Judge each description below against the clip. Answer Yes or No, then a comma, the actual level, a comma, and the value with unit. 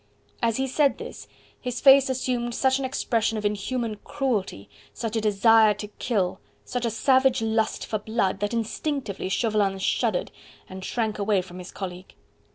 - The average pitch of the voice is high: Yes, high, 225 Hz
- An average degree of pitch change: Yes, average, 3.6 semitones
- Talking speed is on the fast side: No, average, 165 wpm